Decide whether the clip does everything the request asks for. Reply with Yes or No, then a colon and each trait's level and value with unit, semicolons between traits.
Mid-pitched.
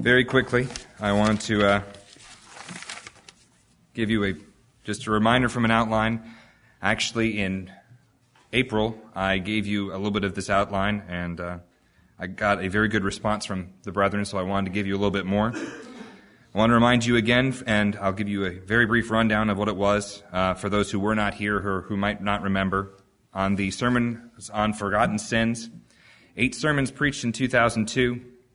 No: low, 105 Hz